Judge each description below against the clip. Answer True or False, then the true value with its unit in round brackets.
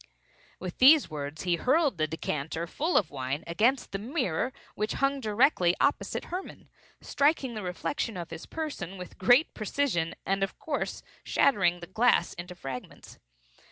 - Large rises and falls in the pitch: True (8.0 semitones)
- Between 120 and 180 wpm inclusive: True (155 wpm)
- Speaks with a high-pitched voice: True (195 Hz)